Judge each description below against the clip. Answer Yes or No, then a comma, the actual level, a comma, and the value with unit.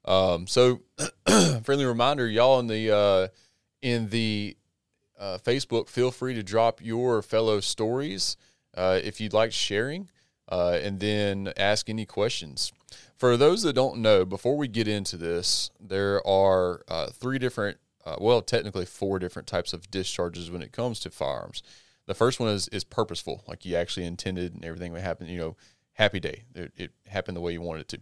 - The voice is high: No, low, 105 Hz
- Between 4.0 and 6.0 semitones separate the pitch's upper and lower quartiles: Yes, average, 4.3 semitones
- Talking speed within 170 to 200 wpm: Yes, average, 180 wpm